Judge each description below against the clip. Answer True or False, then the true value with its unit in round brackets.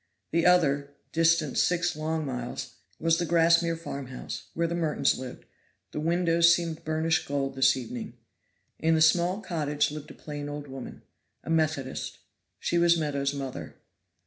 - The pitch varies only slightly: False (3.0 semitones)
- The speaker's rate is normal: True (150 wpm)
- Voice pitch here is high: False (160 Hz)